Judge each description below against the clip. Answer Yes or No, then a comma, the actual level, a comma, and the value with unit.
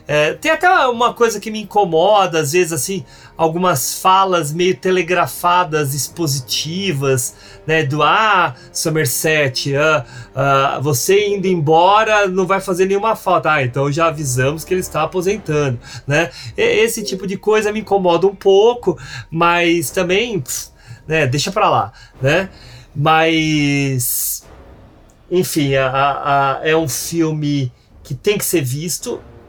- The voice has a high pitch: No, medium, 160 Hz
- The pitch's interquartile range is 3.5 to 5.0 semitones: No, wide, 5.4 semitones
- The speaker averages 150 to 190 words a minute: No, average, 140 wpm